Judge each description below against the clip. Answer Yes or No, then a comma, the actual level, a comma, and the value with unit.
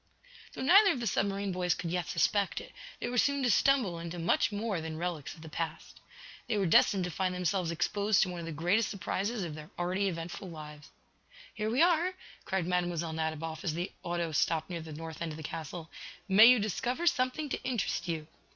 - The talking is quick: Yes, fast, 210 wpm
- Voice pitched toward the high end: No, medium, 180 Hz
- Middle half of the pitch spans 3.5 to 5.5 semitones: Yes, average, 4.5 semitones